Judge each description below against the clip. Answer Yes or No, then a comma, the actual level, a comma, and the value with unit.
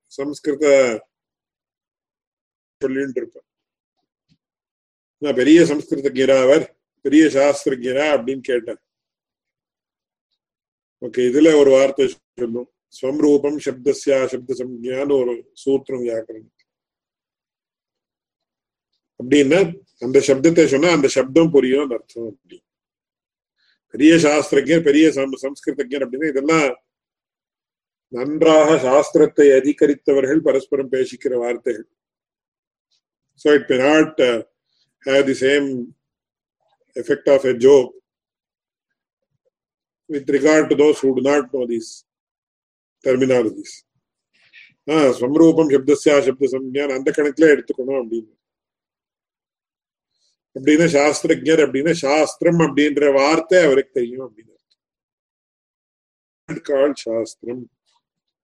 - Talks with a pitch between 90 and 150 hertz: Yes, medium, 140 Hz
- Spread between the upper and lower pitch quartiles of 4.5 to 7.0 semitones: No, average, 2.7 semitones